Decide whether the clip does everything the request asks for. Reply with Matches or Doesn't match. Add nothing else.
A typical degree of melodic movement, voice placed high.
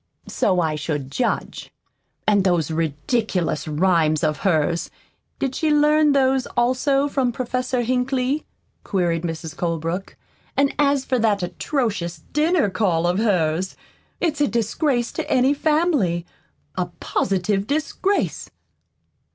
Doesn't match